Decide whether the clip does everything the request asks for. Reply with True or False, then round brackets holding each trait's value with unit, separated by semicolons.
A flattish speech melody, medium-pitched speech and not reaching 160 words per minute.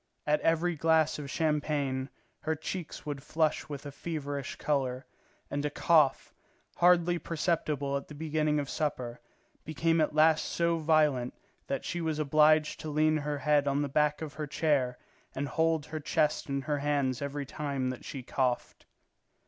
False (2.0 semitones; 150 Hz; 165 wpm)